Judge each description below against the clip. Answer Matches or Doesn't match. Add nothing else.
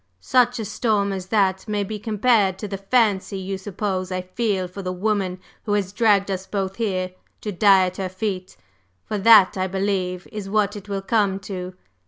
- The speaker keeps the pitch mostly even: Matches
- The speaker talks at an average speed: Matches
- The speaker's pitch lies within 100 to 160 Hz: Doesn't match